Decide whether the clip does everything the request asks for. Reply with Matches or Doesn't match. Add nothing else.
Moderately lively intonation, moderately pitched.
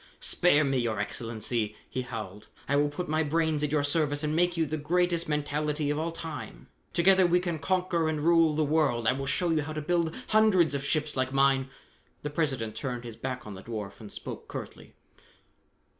Matches